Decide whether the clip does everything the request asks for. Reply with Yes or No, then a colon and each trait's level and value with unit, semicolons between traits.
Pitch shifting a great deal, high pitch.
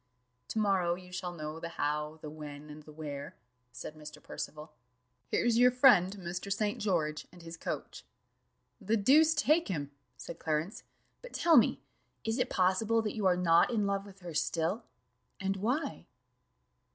No: wide, 5.7 semitones; medium, 180 Hz